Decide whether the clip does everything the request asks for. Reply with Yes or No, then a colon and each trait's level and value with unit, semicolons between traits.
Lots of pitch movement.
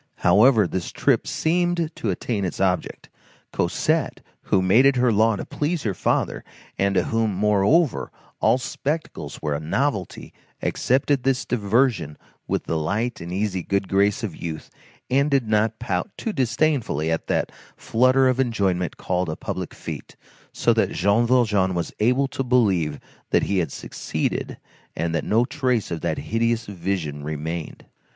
Yes: wide, 5.9 semitones